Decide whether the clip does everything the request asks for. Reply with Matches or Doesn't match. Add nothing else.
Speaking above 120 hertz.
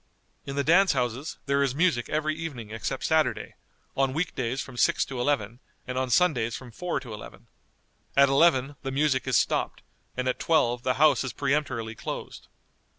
Matches